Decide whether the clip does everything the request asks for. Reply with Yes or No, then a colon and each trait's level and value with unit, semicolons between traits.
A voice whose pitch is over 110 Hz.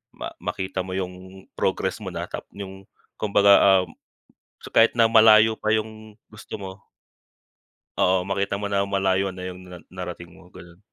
No: very low, 95 Hz